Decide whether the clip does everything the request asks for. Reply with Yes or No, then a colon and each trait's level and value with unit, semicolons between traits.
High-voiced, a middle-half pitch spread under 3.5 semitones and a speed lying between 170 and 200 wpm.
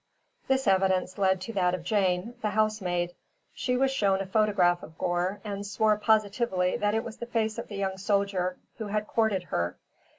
Yes: high, 200 Hz; average, 2.9 semitones; average, 190 wpm